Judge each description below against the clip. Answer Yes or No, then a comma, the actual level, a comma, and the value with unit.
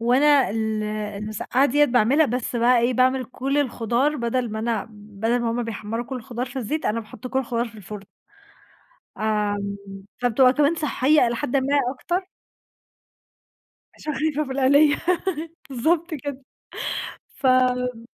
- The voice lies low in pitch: No, very high, 250 Hz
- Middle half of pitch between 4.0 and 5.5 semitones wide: No, average, 3.6 semitones